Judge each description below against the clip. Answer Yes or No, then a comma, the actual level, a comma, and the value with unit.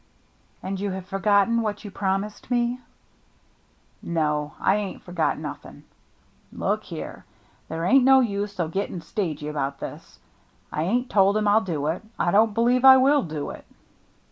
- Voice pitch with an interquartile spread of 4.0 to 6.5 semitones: Yes, average, 5.1 semitones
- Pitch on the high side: Yes, high, 200 Hz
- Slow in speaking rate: No, average, 175 wpm